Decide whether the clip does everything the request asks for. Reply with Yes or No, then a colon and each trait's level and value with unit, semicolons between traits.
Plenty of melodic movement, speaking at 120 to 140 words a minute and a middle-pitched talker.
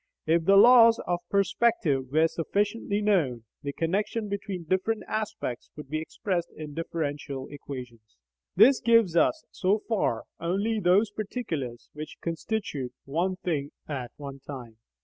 Yes: wide, 6.5 semitones; slow, 135 wpm; medium, 170 Hz